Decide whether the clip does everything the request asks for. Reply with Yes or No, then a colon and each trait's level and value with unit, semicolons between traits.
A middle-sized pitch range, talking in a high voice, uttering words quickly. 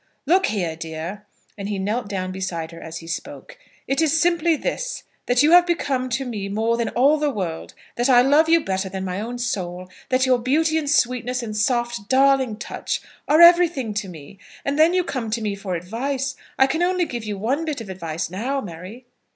No: wide, 6.5 semitones; high, 240 Hz; fast, 210 wpm